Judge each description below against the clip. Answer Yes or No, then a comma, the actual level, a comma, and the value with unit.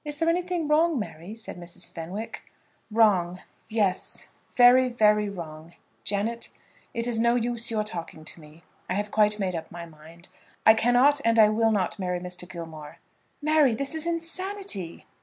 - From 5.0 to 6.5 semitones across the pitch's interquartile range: Yes, wide, 5.6 semitones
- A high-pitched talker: Yes, high, 215 Hz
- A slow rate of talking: No, average, 165 wpm